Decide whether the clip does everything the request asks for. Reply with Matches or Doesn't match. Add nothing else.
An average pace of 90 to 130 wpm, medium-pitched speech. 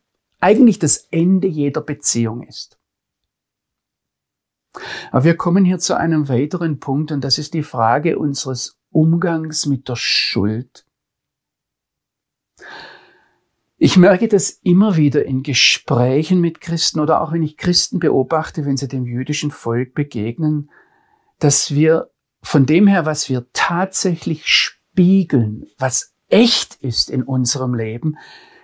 Matches